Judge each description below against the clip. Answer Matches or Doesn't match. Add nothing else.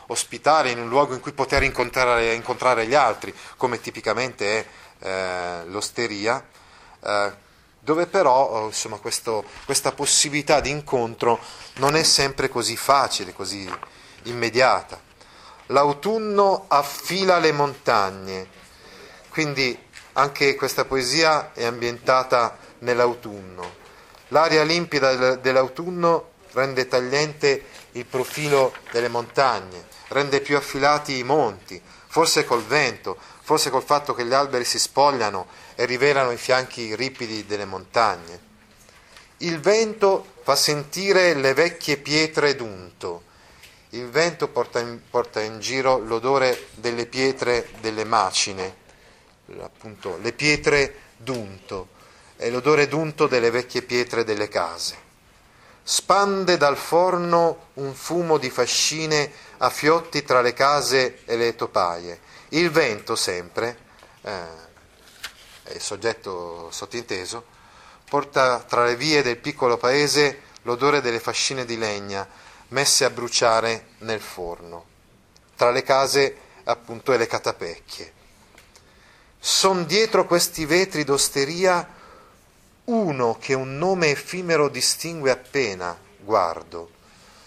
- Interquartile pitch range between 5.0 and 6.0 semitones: Doesn't match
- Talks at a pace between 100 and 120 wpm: Matches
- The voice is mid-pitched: Doesn't match